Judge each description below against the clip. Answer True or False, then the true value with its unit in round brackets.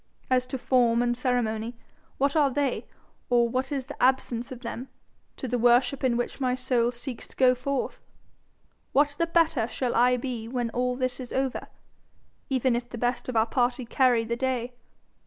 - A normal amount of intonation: False (1.5 semitones)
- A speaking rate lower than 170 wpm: False (185 wpm)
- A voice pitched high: True (250 Hz)